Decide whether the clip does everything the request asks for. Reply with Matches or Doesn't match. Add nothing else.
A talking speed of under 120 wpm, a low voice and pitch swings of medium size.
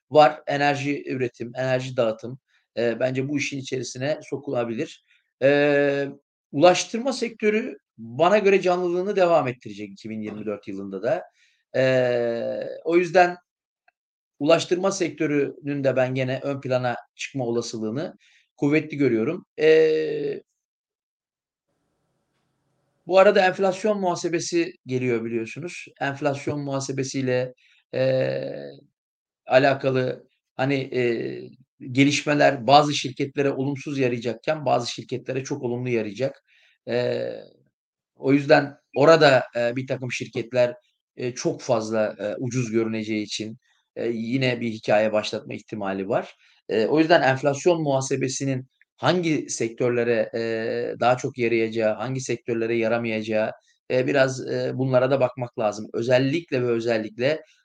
Matches